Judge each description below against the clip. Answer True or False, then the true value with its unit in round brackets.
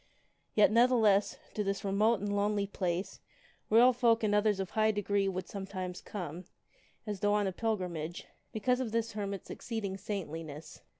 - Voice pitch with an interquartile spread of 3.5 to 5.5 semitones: False (2.4 semitones)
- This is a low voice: False (205 Hz)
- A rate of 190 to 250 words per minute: False (165 wpm)